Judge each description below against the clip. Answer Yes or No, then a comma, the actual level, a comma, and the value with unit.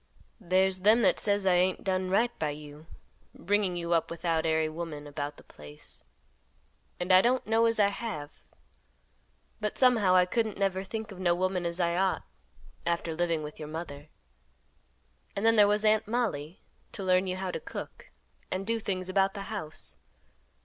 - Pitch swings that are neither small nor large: Yes, average, 3.6 semitones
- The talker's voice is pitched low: No, medium, 185 Hz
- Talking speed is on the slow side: No, average, 175 wpm